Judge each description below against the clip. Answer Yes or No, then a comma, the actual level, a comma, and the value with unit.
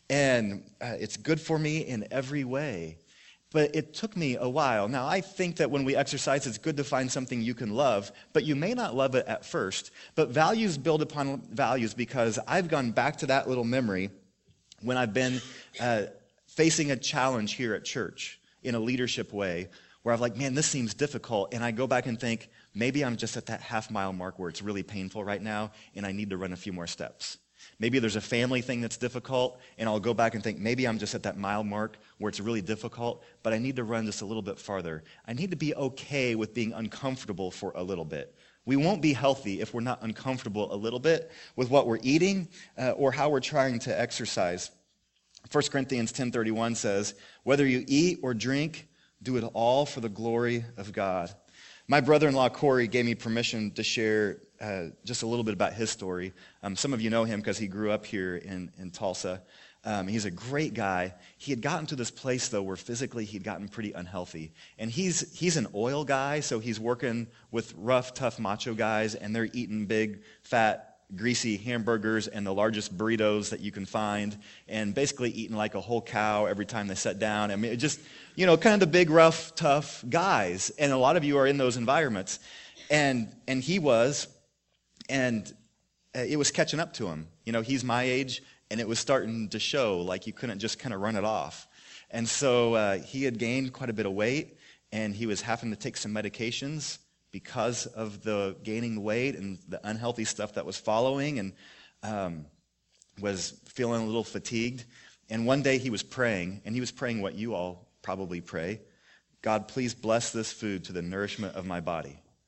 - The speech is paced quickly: Yes, fast, 210 wpm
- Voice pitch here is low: Yes, low, 115 Hz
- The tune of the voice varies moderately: Yes, average, 4.1 semitones